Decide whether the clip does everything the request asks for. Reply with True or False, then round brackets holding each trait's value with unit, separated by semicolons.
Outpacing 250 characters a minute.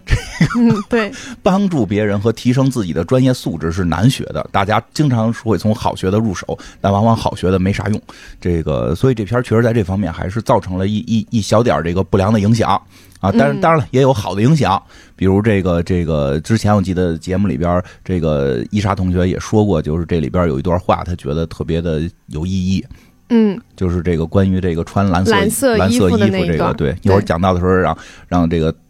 True (320 characters per minute)